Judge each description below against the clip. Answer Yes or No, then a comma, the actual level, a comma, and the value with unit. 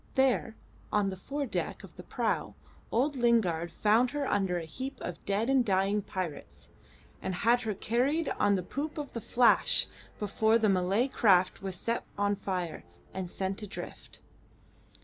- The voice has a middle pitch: No, high, 210 Hz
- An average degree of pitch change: Yes, average, 4.5 semitones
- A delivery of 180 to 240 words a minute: No, average, 165 wpm